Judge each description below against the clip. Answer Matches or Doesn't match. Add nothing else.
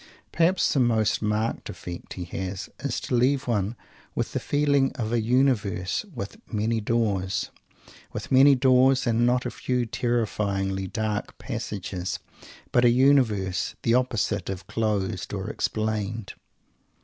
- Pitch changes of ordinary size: Matches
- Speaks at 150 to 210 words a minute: Doesn't match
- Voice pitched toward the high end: Doesn't match